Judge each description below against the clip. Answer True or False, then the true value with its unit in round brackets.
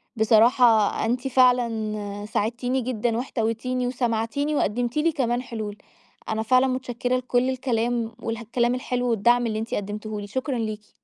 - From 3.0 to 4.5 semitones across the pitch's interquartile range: False (2.4 semitones)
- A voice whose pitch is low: False (240 Hz)